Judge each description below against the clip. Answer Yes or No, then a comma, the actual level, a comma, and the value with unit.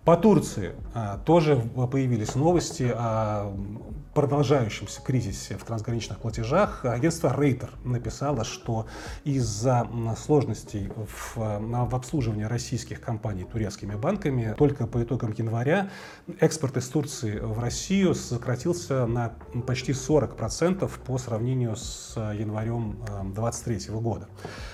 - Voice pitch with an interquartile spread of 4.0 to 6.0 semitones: Yes, average, 4.3 semitones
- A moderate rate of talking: No, slow, 100 wpm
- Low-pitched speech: Yes, low, 120 Hz